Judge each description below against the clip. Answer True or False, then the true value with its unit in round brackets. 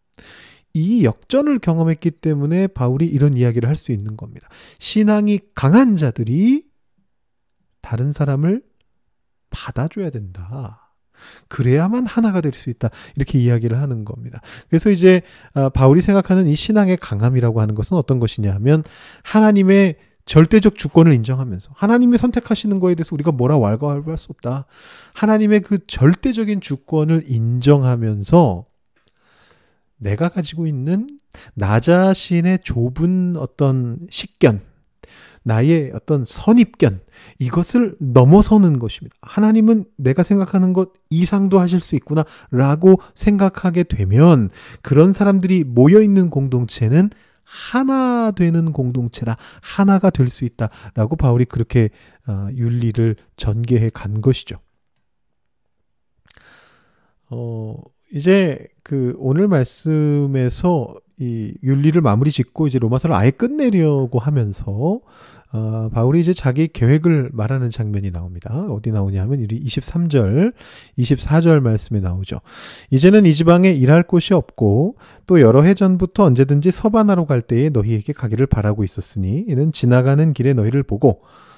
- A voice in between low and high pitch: True (145 Hz)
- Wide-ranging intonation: True (7.3 semitones)